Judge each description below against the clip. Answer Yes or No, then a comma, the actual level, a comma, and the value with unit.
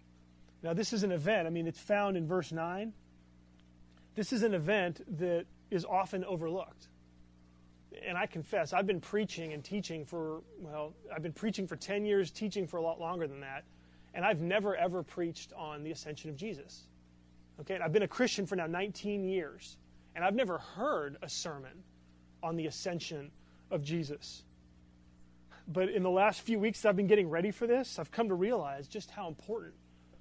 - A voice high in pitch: No, medium, 165 Hz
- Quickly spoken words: No, average, 185 wpm